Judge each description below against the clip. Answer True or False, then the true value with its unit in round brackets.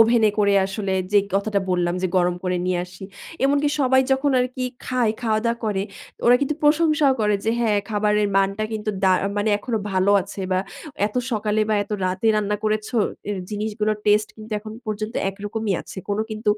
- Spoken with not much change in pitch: True (2.0 semitones)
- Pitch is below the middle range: False (215 Hz)